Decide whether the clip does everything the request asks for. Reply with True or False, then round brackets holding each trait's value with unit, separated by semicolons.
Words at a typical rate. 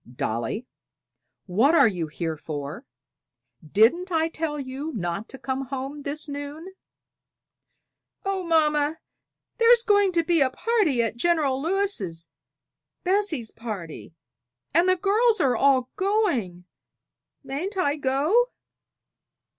False (115 wpm)